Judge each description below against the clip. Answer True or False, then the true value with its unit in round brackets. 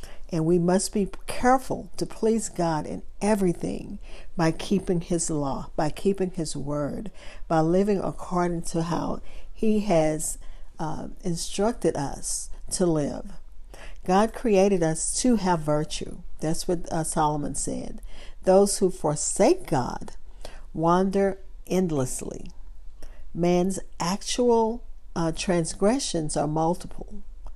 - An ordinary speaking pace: False (115 wpm)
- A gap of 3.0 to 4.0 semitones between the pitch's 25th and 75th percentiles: True (3.7 semitones)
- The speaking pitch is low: False (175 Hz)